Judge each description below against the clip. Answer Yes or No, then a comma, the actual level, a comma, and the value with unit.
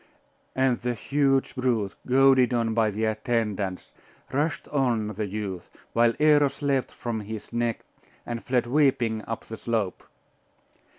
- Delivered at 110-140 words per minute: Yes, slow, 135 wpm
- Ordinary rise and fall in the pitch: Yes, average, 3.3 semitones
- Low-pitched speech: Yes, low, 120 Hz